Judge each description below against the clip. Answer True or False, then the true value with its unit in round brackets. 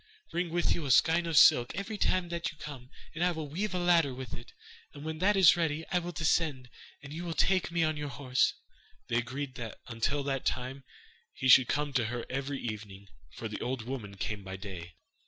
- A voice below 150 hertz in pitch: True (140 Hz)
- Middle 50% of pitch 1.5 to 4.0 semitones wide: False (5.5 semitones)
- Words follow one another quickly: True (220 wpm)